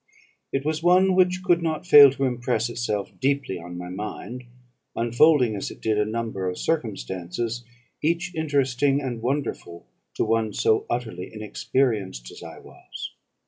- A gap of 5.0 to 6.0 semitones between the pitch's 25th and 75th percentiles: Yes, wide, 5.5 semitones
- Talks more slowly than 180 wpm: Yes, average, 150 wpm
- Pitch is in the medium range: No, low, 120 Hz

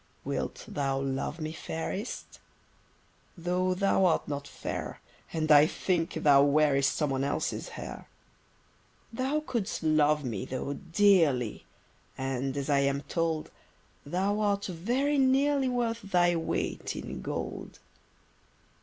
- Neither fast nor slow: No, slow, 120 wpm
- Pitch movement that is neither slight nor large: No, wide, 6.0 semitones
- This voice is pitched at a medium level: Yes, medium, 160 Hz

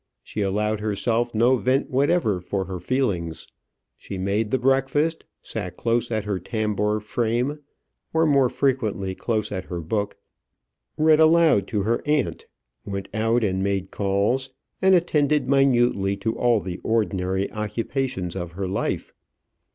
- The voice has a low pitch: Yes, low, 110 Hz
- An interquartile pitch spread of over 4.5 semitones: Yes, average, 5.0 semitones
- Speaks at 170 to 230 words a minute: No, average, 145 wpm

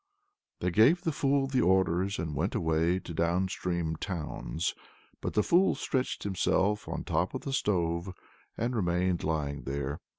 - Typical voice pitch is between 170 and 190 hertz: No, very low, 90 Hz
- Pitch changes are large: No, average, 4.3 semitones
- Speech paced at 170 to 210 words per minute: No, average, 160 wpm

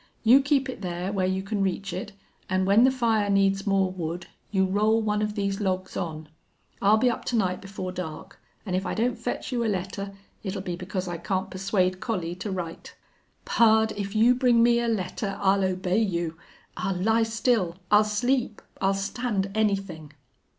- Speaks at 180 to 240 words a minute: Yes, average, 190 wpm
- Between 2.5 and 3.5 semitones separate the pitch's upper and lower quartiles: Yes, average, 2.9 semitones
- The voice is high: Yes, high, 195 Hz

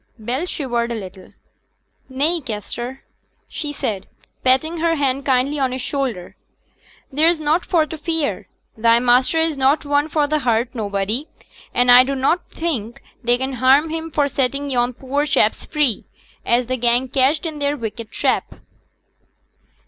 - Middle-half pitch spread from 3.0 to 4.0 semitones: Yes, average, 3.7 semitones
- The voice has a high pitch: Yes, very high, 265 Hz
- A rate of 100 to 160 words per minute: Yes, average, 155 wpm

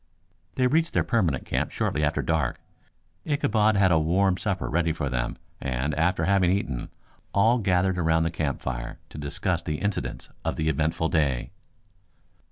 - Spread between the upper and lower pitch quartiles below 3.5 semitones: No, average, 4.5 semitones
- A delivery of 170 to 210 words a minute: No, average, 160 wpm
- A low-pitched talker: Yes, very low, 85 Hz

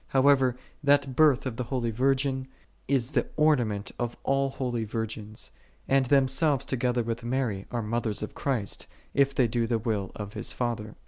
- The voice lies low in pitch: Yes, low, 125 Hz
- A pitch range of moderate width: Yes, average, 3.1 semitones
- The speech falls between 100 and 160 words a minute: No, average, 175 wpm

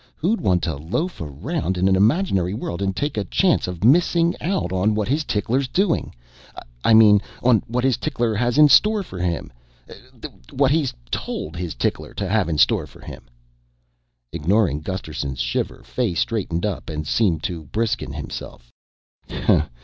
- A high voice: No, low, 105 Hz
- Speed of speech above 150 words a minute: Yes, average, 165 wpm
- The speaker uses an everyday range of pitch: No, wide, 7.3 semitones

